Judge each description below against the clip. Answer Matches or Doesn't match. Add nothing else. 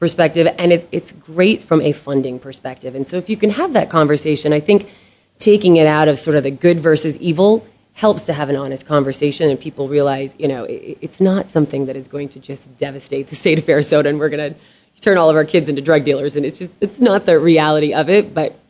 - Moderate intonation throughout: Matches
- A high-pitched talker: Doesn't match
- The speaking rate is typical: Doesn't match